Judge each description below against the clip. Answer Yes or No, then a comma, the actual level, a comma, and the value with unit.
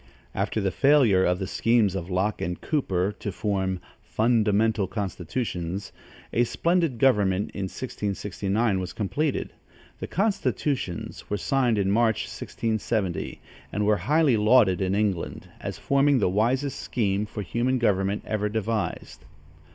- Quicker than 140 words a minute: No, slow, 135 wpm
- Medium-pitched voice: No, low, 105 Hz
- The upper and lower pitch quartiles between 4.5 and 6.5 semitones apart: No, average, 3.8 semitones